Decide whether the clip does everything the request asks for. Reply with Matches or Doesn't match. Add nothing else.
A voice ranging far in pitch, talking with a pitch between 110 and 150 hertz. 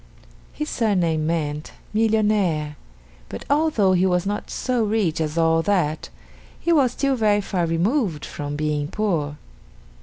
Doesn't match